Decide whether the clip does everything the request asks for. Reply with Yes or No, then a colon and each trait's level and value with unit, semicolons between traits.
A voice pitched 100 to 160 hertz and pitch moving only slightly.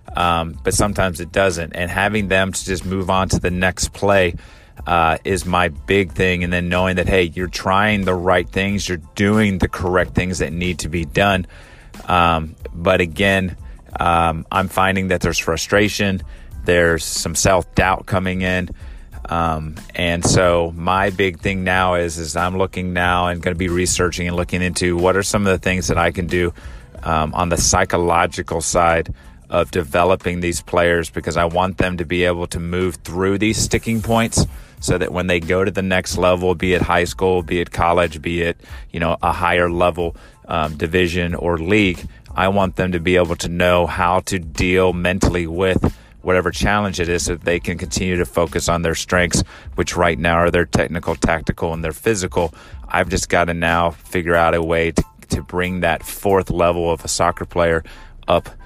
No: very low, 90 Hz; narrow, 1.7 semitones